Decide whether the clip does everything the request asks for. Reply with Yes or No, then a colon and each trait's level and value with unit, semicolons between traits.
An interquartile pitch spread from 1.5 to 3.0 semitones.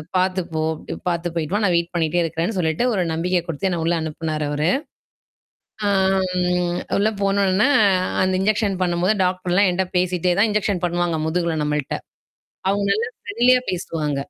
Yes: narrow, 2.6 semitones